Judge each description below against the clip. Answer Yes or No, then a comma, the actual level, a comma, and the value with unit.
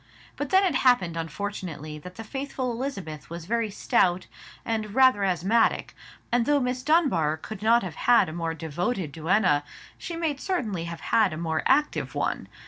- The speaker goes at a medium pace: Yes, average, 170 wpm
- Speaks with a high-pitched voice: Yes, high, 205 Hz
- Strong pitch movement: Yes, wide, 7.2 semitones